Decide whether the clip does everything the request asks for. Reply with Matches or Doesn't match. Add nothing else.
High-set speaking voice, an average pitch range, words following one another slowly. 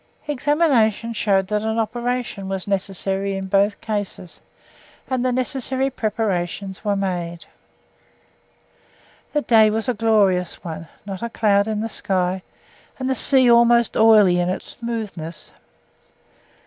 Matches